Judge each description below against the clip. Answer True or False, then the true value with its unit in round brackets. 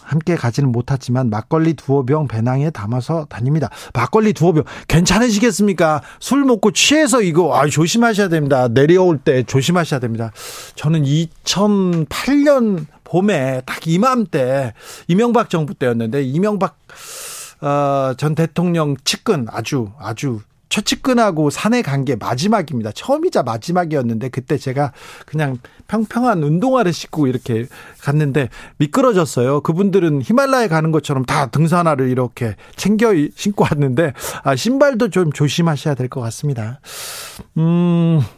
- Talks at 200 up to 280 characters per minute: False (310 characters per minute)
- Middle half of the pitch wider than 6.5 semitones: False (6.2 semitones)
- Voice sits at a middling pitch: True (155 Hz)